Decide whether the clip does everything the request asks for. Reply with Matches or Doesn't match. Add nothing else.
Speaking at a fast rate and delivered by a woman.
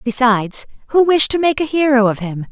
Matches